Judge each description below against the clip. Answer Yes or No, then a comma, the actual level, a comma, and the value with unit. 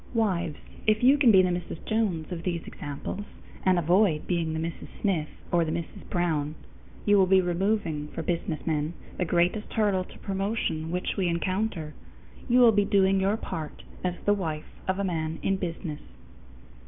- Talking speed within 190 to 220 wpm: No, average, 175 wpm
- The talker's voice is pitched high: No, medium, 180 Hz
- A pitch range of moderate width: Yes, average, 3.4 semitones